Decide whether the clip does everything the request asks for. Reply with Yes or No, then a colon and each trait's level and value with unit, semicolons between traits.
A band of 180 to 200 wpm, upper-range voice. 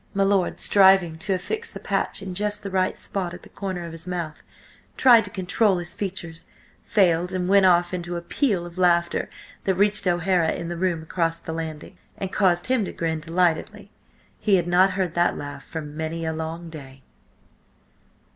No: average, 190 wpm; medium, 175 Hz